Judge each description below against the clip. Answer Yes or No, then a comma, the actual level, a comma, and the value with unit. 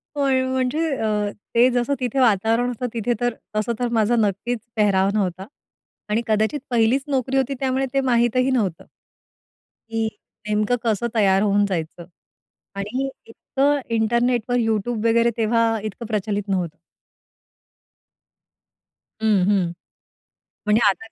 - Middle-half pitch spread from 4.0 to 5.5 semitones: No, average, 3.0 semitones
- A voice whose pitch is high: Yes, high, 225 Hz